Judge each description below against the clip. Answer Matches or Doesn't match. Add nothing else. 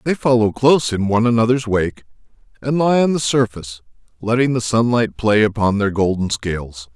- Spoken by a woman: Doesn't match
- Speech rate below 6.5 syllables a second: Matches